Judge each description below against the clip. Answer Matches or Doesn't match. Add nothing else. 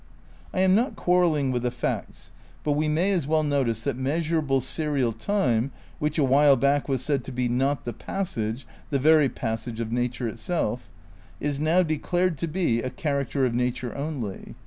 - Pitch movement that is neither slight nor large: Matches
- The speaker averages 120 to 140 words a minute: Doesn't match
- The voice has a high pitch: Doesn't match